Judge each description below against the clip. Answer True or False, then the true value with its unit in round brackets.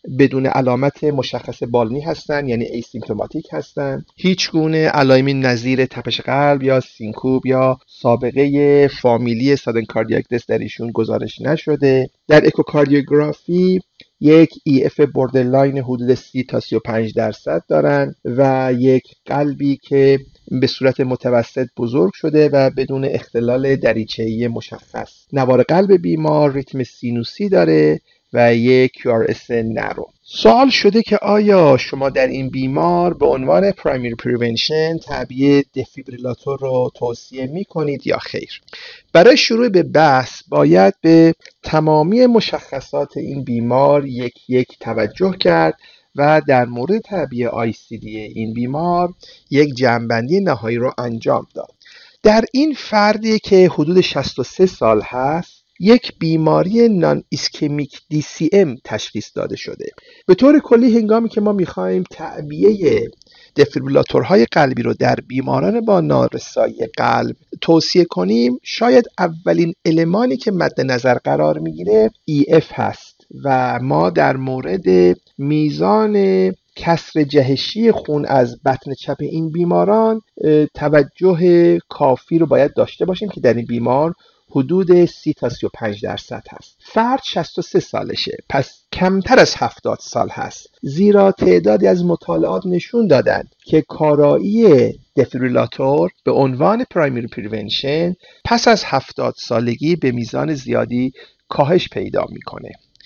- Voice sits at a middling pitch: True (145 Hz)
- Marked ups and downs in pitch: True (5.8 semitones)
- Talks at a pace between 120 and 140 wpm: True (125 wpm)